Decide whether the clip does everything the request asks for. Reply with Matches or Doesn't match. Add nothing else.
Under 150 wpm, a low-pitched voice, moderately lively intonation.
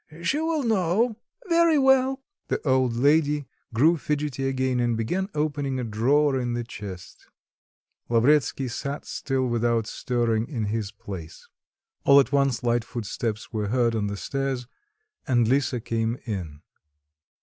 Matches